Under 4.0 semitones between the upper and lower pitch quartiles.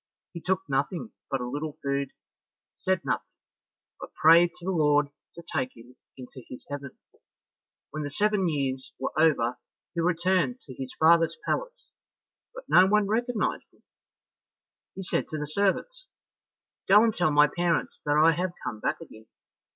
No: average, 5.1 semitones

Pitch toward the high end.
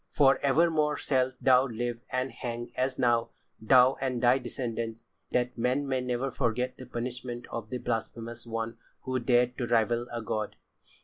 No: low, 125 Hz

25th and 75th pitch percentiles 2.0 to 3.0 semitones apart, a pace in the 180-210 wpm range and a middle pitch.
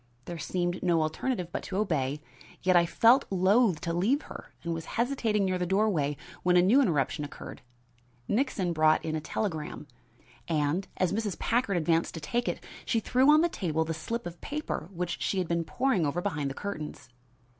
No: average, 5.0 semitones; average, 190 wpm; medium, 180 Hz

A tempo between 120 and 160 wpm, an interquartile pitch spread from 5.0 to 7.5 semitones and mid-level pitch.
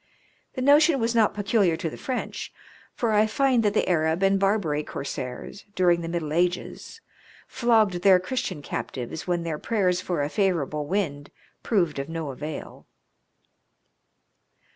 Yes: average, 145 wpm; average, 5.3 semitones; medium, 180 Hz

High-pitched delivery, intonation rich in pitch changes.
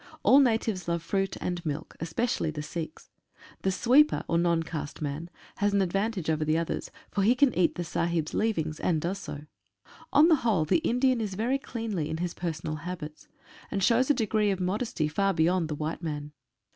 No: medium, 180 Hz; wide, 5.7 semitones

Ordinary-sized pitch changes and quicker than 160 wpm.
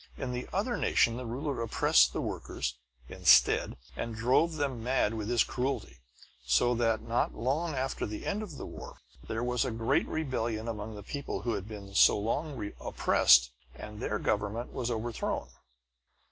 Yes: average, 3.6 semitones; average, 170 wpm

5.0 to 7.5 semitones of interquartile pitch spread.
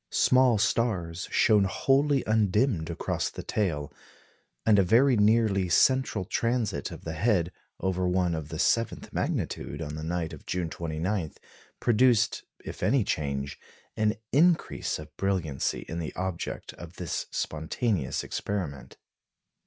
Yes: wide, 5.5 semitones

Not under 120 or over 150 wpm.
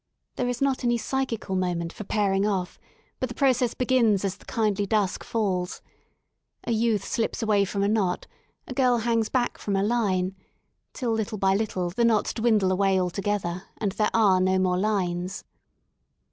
No: average, 175 wpm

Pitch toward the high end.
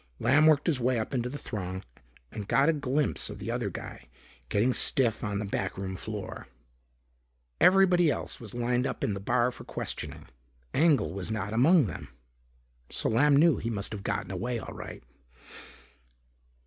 No: low, 120 Hz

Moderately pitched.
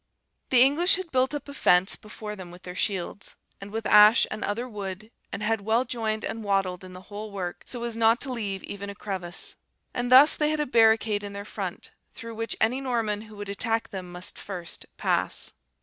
No: high, 215 Hz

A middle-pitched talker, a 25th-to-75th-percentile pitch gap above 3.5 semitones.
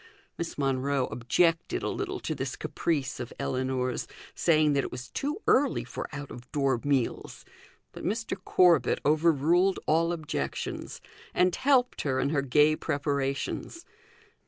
Yes: medium, 145 Hz; average, 4.2 semitones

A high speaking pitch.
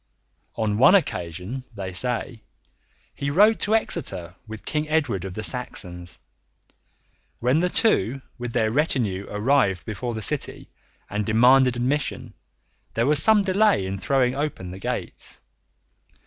No: low, 120 Hz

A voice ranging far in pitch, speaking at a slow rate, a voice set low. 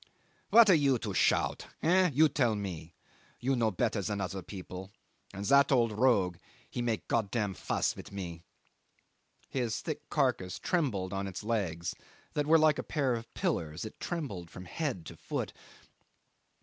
No: wide, 6.7 semitones; average, 160 wpm; low, 110 Hz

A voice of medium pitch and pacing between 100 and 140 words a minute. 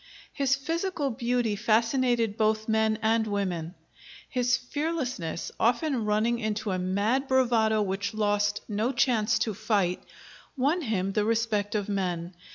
No: high, 220 Hz; slow, 135 wpm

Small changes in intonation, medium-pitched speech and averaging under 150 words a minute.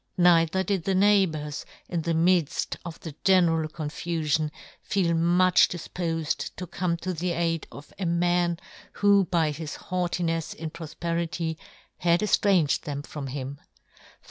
Yes: narrow, 2.1 semitones; medium, 170 Hz; average, 140 wpm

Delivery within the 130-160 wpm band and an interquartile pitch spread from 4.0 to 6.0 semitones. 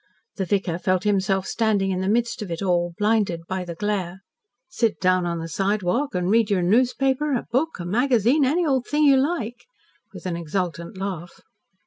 No: average, 185 wpm; average, 5.1 semitones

